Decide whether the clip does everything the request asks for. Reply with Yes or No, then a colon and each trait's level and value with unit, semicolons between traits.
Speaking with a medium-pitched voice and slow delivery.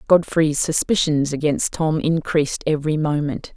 Yes: medium, 150 Hz; slow, 120 wpm